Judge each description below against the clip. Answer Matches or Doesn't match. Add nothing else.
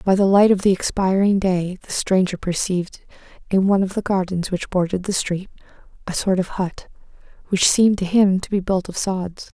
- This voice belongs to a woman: Matches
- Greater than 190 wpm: Matches